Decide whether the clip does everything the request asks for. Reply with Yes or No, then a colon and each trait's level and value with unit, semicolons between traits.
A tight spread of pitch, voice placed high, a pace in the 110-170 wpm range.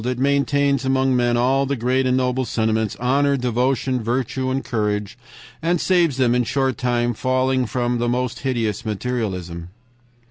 No: narrow, 1.9 semitones; low, 125 Hz; average, 155 wpm